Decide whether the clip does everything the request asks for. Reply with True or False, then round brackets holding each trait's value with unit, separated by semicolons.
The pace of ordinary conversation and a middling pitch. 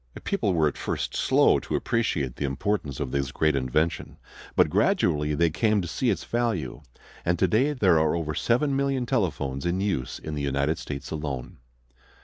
False (175 wpm; 80 Hz)